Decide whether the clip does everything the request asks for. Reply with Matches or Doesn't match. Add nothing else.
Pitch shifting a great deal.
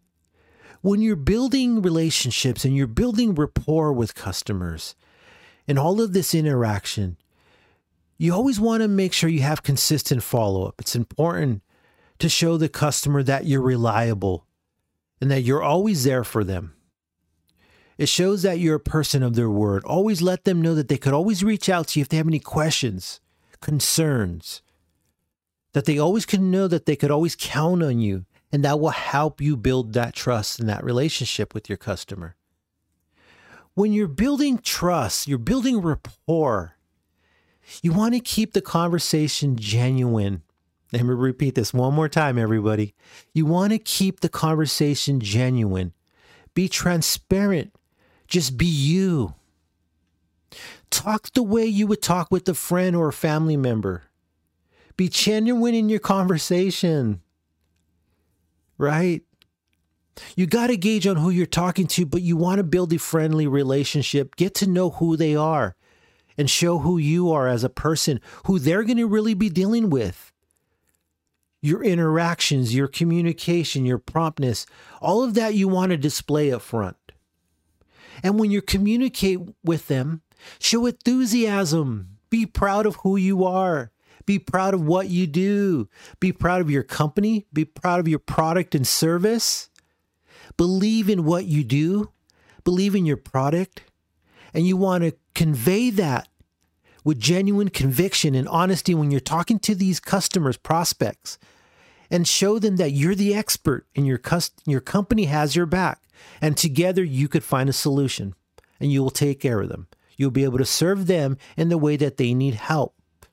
Matches